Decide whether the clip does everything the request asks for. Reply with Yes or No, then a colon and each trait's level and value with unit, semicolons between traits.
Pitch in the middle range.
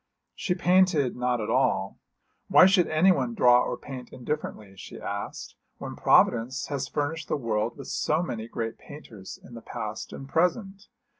No: low, 130 Hz